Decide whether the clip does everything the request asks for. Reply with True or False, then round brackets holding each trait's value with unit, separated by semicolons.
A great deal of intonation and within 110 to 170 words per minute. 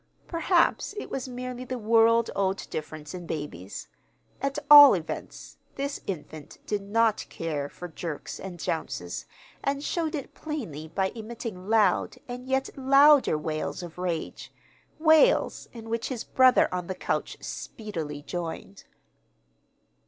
True (7.9 semitones; 135 wpm)